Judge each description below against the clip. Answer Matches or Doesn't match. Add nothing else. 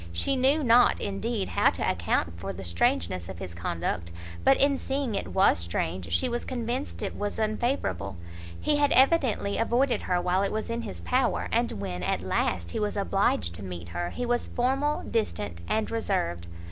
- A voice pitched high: Matches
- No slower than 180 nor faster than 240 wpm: Matches